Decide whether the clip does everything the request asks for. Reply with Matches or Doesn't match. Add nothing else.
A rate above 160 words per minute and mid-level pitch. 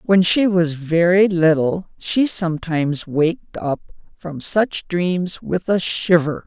Doesn't match